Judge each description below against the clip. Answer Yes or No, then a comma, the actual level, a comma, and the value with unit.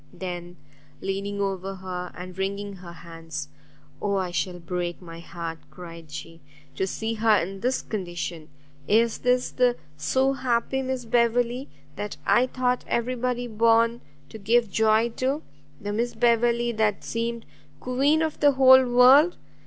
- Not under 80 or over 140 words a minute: No, average, 150 wpm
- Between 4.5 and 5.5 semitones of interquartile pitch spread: Yes, average, 5.1 semitones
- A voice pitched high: Yes, high, 220 Hz